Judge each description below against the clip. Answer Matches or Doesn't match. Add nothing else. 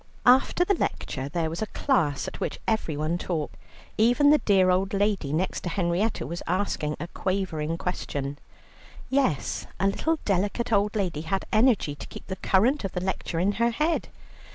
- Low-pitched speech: Doesn't match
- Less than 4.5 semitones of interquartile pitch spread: Doesn't match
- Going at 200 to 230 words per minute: Doesn't match